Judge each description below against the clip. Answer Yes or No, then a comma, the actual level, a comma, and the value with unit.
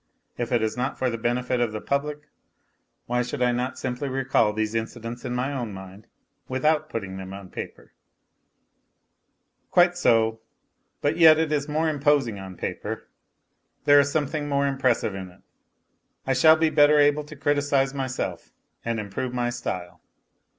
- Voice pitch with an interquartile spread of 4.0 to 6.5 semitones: Yes, average, 4.3 semitones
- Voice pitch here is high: No, low, 130 Hz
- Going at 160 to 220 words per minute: Yes, average, 165 wpm